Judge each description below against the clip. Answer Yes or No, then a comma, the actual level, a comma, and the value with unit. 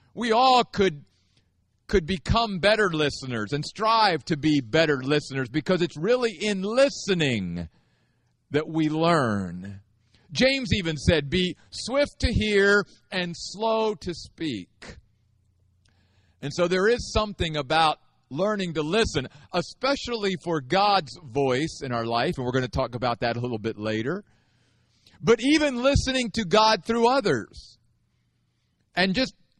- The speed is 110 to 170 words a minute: Yes, average, 140 wpm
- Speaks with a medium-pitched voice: Yes, medium, 160 Hz